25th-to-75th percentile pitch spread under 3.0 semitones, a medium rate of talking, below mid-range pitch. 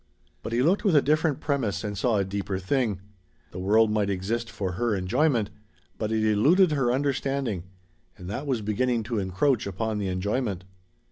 No: average, 5.0 semitones; average, 180 wpm; low, 110 Hz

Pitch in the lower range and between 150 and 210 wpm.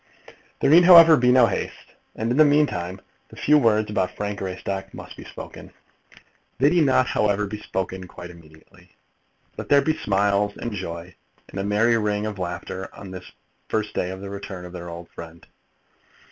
Yes: low, 100 Hz; average, 190 wpm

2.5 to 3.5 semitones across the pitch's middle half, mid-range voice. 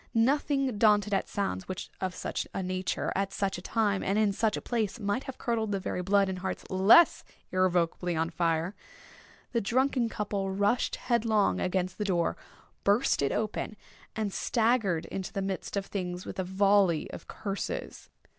No: average, 2.9 semitones; high, 200 Hz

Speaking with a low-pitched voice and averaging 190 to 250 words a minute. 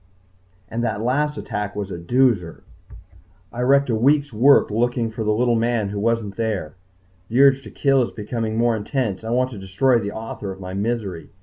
Yes: low, 115 Hz; average, 195 wpm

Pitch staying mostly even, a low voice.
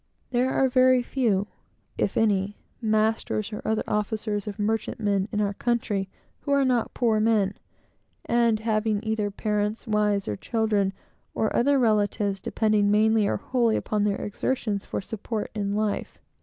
No: narrow, 1.7 semitones; high, 215 Hz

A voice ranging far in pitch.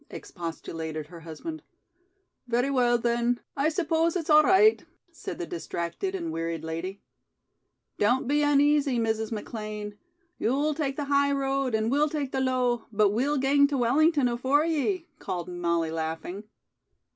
Yes: wide, 6.0 semitones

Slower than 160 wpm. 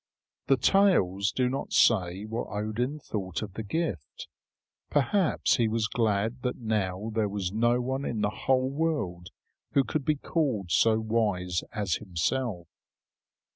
Yes: average, 145 wpm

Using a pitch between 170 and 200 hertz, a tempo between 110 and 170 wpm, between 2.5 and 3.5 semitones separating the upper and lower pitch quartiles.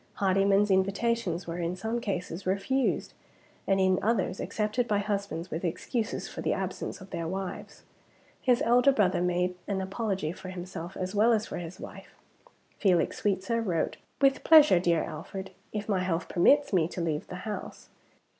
Yes: high, 190 Hz; average, 165 wpm; average, 3.2 semitones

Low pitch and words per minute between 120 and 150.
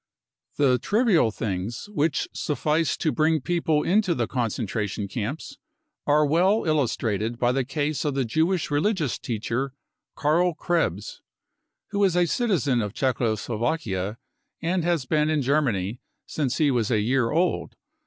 No: medium, 145 Hz; average, 145 wpm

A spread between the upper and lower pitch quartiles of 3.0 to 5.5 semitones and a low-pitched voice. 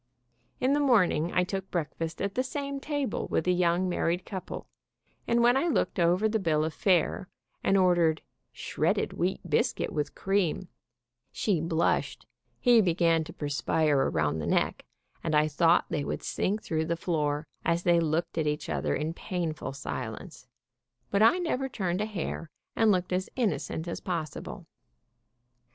No: average, 4.0 semitones; medium, 175 Hz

